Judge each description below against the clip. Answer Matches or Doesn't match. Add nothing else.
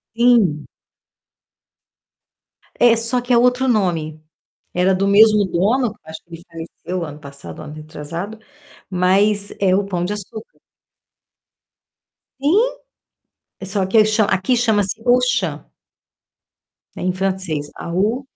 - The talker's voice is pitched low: Doesn't match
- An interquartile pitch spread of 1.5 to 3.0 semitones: Doesn't match